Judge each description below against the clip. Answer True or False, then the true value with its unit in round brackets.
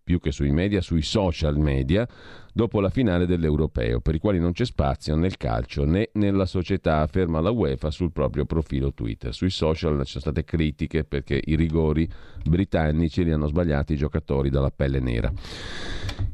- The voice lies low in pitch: True (80 Hz)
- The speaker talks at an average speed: False (175 wpm)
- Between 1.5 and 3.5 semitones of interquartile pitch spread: False (3.9 semitones)